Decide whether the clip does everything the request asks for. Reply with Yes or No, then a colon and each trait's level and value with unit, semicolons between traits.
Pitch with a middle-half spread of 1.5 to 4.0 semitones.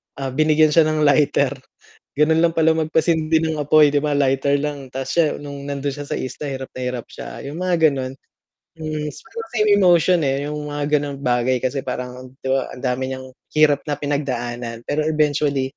Yes: narrow, 2.6 semitones